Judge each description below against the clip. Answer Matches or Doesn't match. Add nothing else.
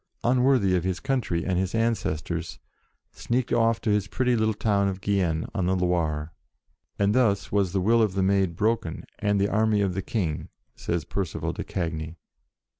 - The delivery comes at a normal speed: Matches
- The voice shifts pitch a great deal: Doesn't match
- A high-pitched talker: Doesn't match